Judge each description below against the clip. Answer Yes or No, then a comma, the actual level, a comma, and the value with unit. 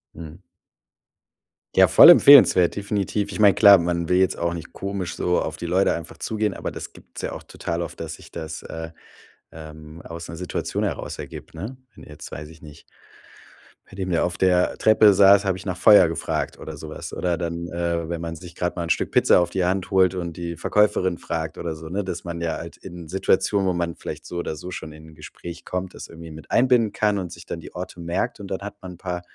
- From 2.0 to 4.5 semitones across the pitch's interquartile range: Yes, narrow, 2.4 semitones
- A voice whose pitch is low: Yes, very low, 85 Hz